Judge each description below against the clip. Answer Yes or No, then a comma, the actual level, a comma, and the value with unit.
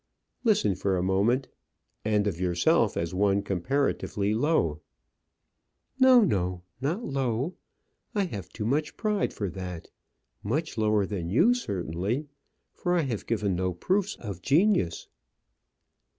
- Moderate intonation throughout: No, wide, 8.5 semitones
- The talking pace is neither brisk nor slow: No, slow, 130 wpm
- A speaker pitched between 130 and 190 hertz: No, low, 105 Hz